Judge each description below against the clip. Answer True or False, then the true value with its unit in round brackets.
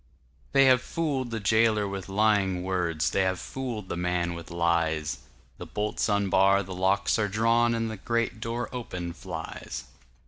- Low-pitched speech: True (100 Hz)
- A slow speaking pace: False (145 wpm)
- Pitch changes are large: False (4.3 semitones)